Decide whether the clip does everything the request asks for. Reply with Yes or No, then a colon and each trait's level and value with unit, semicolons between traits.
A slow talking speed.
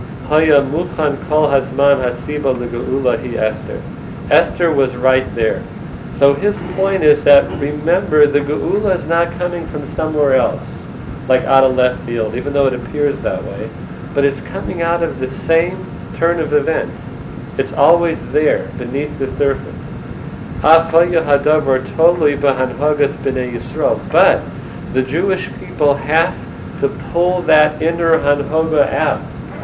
Yes: slow, 125 wpm